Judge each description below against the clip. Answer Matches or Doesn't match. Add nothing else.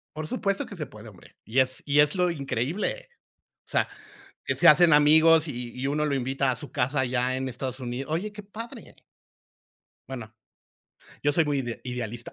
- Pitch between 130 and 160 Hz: Matches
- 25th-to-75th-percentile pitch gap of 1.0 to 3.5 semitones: Doesn't match